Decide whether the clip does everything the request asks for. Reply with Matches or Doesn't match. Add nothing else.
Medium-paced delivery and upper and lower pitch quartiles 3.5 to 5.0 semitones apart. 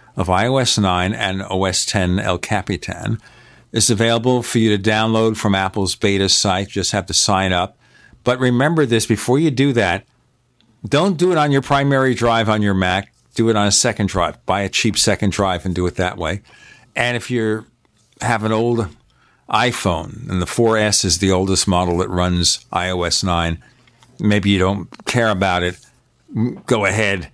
Matches